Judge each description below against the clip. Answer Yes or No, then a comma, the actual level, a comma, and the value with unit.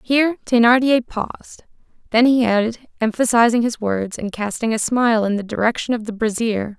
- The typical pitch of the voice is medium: No, high, 230 Hz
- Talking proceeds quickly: No, average, 170 wpm